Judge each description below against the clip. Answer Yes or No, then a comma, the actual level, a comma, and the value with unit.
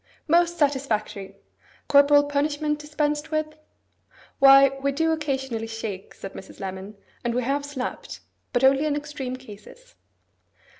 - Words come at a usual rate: No, slow, 130 wpm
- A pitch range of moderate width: Yes, average, 3.7 semitones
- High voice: Yes, very high, 280 Hz